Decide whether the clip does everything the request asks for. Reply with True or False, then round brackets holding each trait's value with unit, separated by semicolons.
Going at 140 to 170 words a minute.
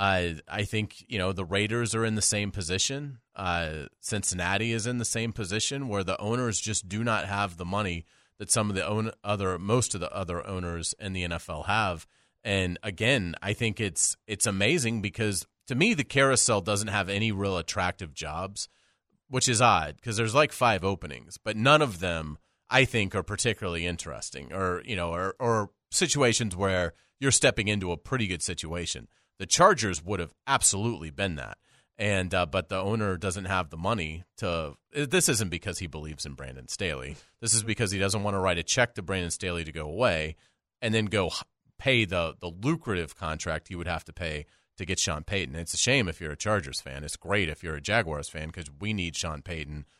False (205 wpm)